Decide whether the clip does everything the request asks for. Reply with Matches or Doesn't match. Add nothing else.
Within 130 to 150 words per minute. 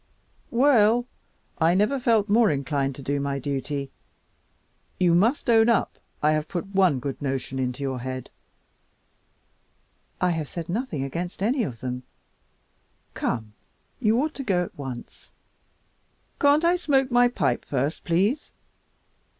Matches